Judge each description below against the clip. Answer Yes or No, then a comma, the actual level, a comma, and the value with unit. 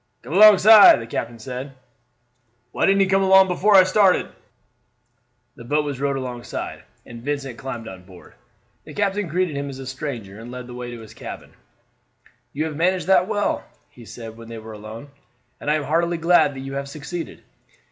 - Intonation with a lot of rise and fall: Yes, wide, 7.2 semitones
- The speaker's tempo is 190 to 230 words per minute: Yes, average, 195 wpm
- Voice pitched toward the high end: No, medium, 140 Hz